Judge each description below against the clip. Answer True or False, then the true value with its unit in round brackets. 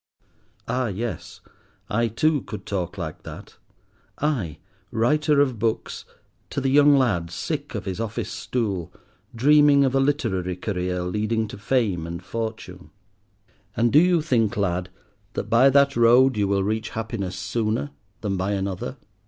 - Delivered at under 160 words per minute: True (145 wpm)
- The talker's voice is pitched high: False (115 Hz)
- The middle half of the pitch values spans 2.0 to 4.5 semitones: False (5.3 semitones)